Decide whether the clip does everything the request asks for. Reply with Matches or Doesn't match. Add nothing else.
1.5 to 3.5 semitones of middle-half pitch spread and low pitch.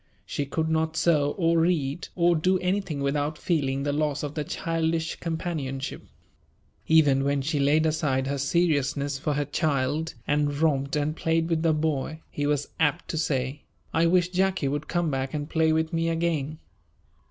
Doesn't match